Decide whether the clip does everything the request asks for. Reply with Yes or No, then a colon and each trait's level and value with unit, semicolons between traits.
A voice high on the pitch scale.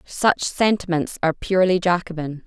No: medium, 175 Hz